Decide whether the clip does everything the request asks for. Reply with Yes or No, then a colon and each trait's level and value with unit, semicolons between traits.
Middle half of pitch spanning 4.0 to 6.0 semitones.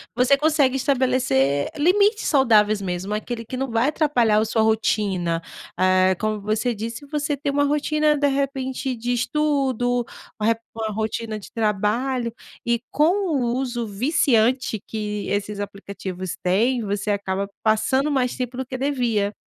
Yes: average, 4.4 semitones